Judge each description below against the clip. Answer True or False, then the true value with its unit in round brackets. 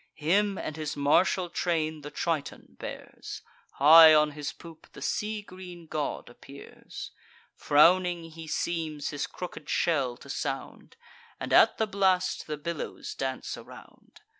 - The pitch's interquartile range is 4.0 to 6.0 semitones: False (3.2 semitones)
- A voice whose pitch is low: False (160 Hz)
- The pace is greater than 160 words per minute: False (140 wpm)